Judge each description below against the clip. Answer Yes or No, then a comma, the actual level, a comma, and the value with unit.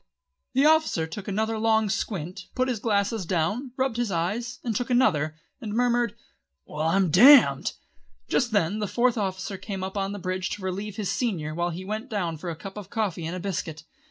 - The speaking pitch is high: Yes, high, 200 Hz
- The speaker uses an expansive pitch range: No, average, 4.1 semitones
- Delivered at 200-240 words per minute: Yes, fast, 205 wpm